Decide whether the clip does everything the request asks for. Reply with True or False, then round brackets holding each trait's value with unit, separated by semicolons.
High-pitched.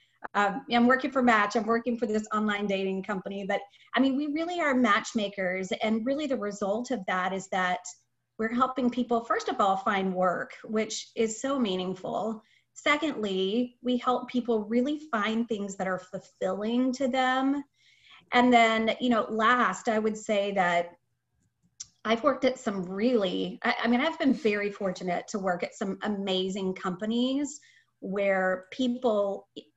True (220 Hz)